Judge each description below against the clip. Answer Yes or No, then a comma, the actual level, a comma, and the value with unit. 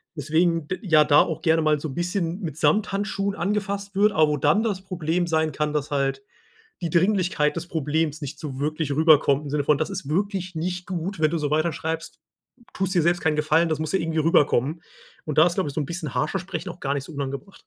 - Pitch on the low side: No, medium, 160 Hz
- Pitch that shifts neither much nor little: Yes, average, 3.3 semitones